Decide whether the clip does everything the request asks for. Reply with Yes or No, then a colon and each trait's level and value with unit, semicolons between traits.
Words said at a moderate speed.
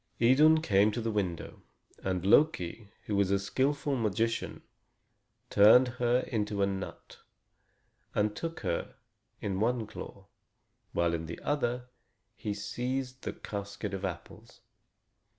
No: slow, 130 wpm